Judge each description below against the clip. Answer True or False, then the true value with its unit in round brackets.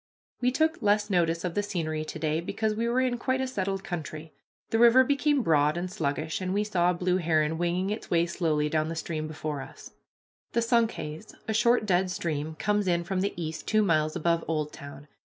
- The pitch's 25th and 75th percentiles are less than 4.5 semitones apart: False (5.2 semitones)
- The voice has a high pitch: False (175 Hz)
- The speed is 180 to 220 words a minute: True (205 wpm)